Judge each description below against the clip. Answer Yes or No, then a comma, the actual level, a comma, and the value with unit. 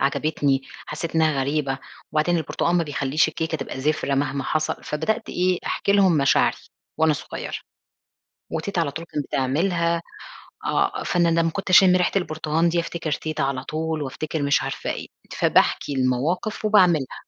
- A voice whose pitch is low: No, medium, 160 Hz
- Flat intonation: No, average, 3.2 semitones